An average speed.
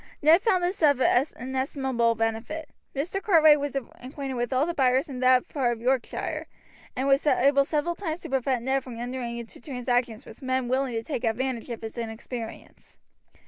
Yes: average, 180 wpm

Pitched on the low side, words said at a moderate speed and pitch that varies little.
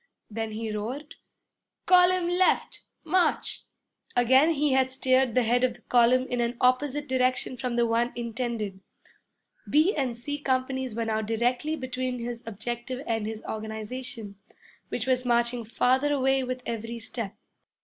No: very high, 250 Hz; average, 150 wpm; narrow, 2.3 semitones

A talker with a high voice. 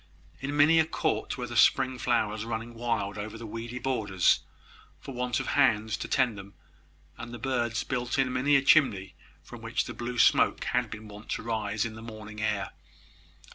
No: low, 115 Hz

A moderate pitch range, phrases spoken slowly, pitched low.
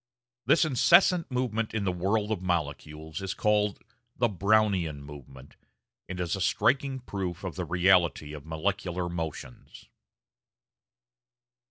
Yes: average, 5.0 semitones; slow, 125 wpm; very low, 95 Hz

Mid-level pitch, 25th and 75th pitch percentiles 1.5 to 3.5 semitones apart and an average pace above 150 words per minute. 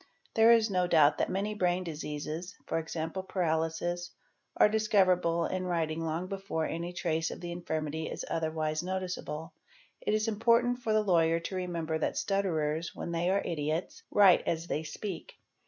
Yes: medium, 175 Hz; average, 3.0 semitones; average, 165 wpm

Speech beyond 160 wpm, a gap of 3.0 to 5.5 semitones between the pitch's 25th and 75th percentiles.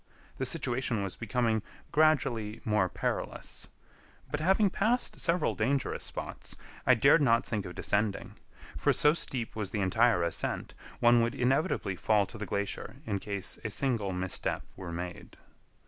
No: average, 150 wpm; average, 4.8 semitones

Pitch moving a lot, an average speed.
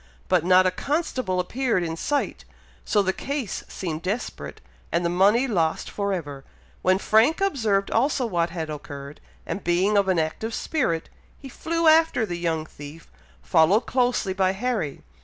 Yes: wide, 6.5 semitones; average, 160 wpm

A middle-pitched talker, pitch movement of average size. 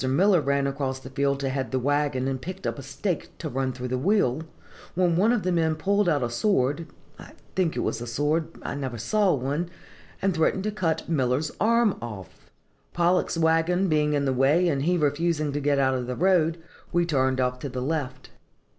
Yes: medium, 145 Hz; average, 4.7 semitones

